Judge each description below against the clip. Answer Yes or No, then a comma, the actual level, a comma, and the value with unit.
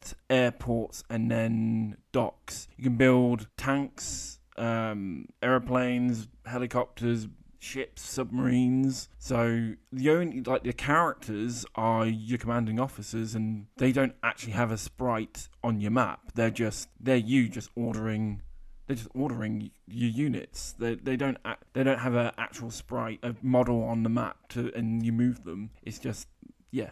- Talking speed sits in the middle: Yes, average, 150 wpm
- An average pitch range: No, narrow, 2.2 semitones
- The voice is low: Yes, low, 120 Hz